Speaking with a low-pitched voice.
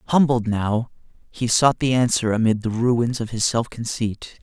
Yes: low, 115 Hz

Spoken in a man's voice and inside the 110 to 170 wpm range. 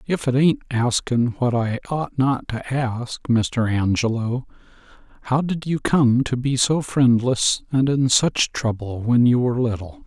Yes: male; average, 165 wpm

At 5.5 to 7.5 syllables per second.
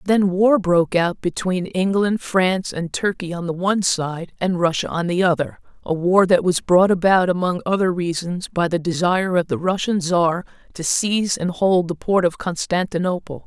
No: 4.9 syllables/s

